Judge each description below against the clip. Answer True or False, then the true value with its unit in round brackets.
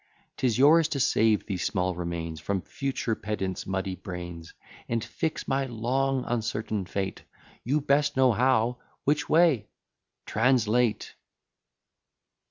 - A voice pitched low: True (115 Hz)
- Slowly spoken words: True (120 wpm)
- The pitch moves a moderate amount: False (5.7 semitones)